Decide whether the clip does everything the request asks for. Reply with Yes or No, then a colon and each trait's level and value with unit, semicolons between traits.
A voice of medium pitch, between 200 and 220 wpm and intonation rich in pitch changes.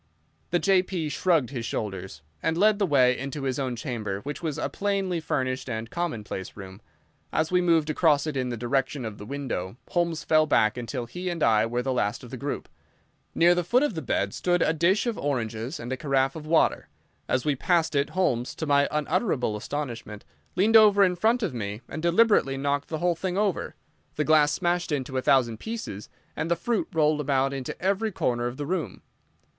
Yes: medium, 145 Hz; fast, 205 wpm; wide, 6.0 semitones